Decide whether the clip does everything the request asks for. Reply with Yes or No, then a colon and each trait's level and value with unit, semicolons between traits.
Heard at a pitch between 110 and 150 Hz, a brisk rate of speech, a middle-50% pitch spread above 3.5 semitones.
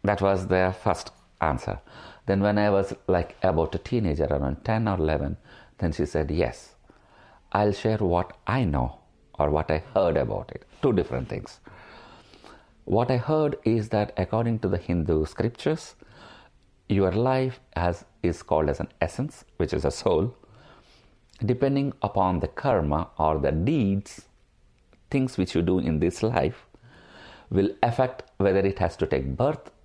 No: very low, 95 Hz; fast, 160 wpm; average, 4.9 semitones